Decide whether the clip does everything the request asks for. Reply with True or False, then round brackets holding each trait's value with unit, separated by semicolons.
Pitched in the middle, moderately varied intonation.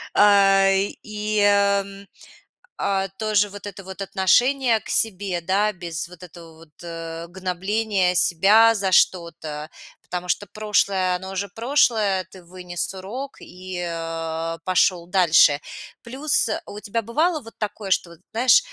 False (195 Hz; 3.1 semitones)